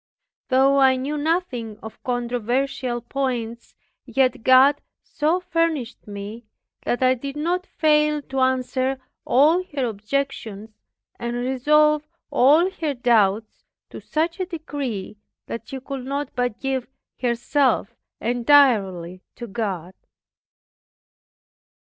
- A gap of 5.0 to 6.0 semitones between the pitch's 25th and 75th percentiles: No, average, 3.6 semitones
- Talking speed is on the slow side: Yes, slow, 115 wpm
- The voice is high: Yes, very high, 260 Hz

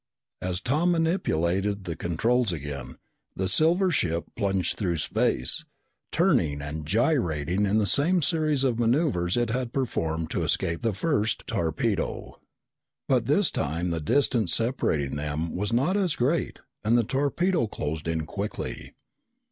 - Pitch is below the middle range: Yes, low, 105 Hz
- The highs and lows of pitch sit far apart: Yes, wide, 8.6 semitones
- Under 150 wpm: Yes, average, 140 wpm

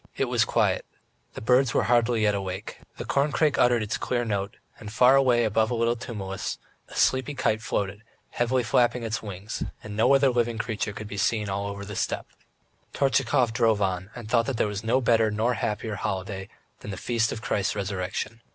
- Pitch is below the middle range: Yes, low, 110 Hz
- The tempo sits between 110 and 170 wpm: No, average, 195 wpm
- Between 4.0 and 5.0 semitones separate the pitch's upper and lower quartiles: No, average, 2.9 semitones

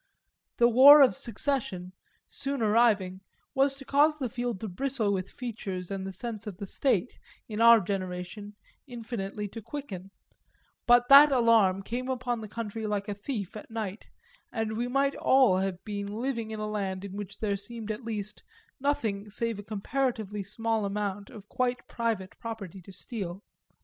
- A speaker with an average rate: Yes, average, 170 wpm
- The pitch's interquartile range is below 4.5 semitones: Yes, average, 3.5 semitones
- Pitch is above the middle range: Yes, high, 220 Hz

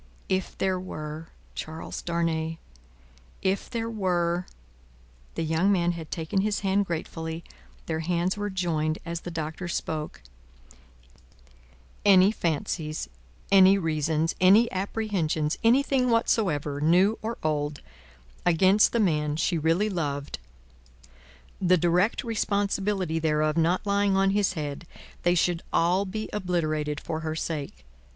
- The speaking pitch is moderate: Yes, medium, 170 Hz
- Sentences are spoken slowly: Yes, slow, 130 wpm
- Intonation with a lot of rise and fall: No, average, 3.8 semitones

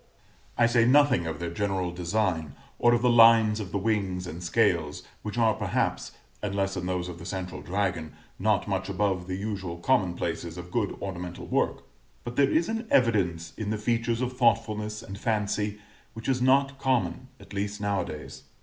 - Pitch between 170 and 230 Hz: No, low, 100 Hz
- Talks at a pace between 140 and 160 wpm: No, average, 185 wpm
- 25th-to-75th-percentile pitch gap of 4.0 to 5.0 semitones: Yes, average, 4.3 semitones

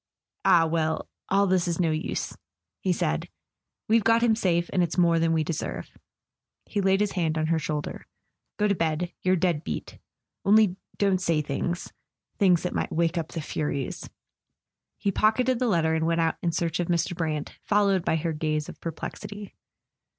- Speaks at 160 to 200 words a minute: Yes, average, 185 wpm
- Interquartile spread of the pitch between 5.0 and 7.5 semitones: No, average, 3.3 semitones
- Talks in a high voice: No, medium, 170 Hz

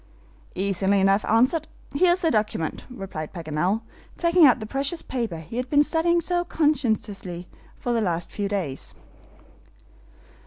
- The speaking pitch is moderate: No, high, 225 Hz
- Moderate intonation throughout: No, wide, 7.5 semitones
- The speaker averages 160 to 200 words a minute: No, average, 145 wpm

